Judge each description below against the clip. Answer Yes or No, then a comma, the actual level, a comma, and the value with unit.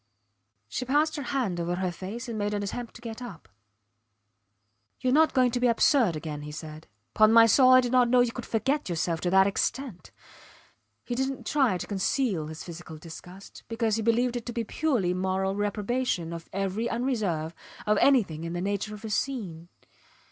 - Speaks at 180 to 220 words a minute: Yes, average, 195 wpm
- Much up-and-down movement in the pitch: Yes, wide, 5.7 semitones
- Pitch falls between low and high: No, high, 215 Hz